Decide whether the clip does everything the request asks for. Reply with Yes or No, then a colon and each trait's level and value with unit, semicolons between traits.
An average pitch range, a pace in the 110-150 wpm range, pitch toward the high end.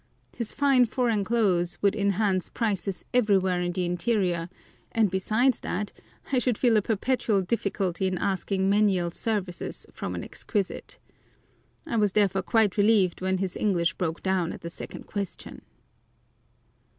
Yes: average, 3.1 semitones; average, 145 wpm; high, 195 Hz